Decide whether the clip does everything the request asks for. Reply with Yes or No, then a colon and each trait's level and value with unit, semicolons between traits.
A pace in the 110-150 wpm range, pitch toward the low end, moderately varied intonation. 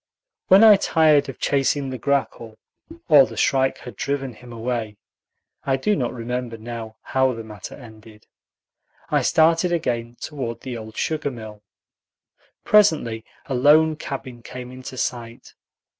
Yes: average, 145 wpm; low, 125 Hz; average, 3.6 semitones